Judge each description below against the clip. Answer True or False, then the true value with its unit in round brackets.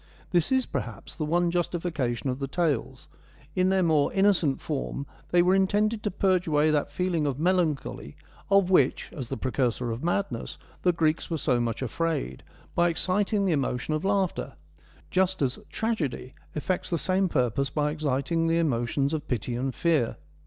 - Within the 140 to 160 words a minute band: False (170 wpm)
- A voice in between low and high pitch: True (160 Hz)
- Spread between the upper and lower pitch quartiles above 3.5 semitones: True (5.3 semitones)